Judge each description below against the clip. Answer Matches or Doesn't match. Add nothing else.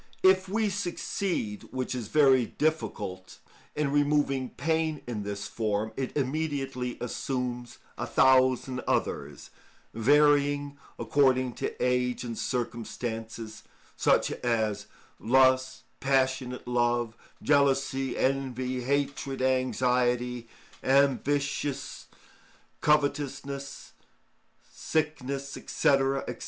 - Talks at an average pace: Doesn't match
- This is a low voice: Matches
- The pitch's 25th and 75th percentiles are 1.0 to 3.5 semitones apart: Matches